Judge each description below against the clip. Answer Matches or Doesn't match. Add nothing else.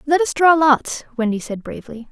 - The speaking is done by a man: Doesn't match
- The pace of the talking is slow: Doesn't match